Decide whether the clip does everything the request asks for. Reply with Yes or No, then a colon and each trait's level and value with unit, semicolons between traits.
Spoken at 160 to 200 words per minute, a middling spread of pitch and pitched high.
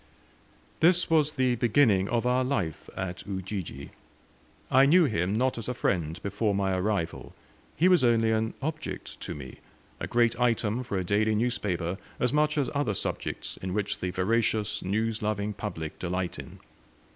No: average, 165 wpm; average, 4.9 semitones; low, 110 Hz